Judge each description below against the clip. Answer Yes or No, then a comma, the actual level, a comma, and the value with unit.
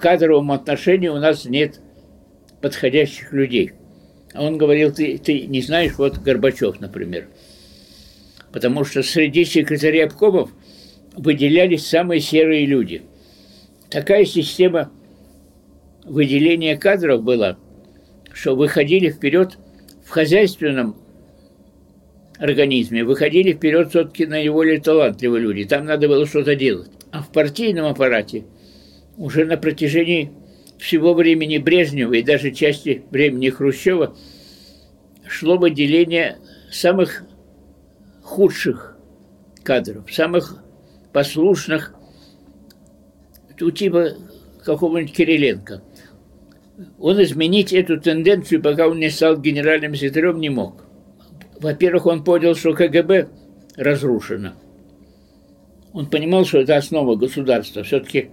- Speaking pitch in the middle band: Yes, medium, 145 Hz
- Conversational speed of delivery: No, slow, 100 wpm